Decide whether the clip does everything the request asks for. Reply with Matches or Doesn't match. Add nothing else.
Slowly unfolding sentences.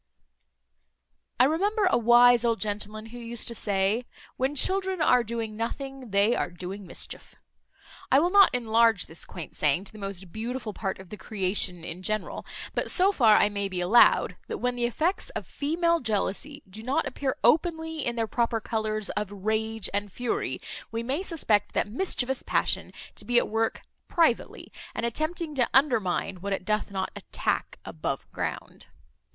Doesn't match